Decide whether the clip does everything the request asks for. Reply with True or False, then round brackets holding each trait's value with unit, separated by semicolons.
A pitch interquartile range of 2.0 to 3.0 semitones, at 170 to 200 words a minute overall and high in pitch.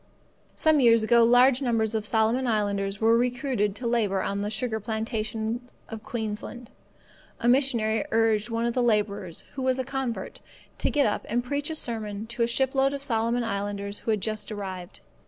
True (2.7 semitones; 180 wpm; 225 Hz)